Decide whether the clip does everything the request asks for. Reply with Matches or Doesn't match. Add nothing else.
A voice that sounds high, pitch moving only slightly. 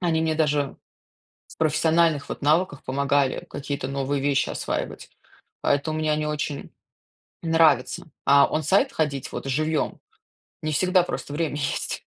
Doesn't match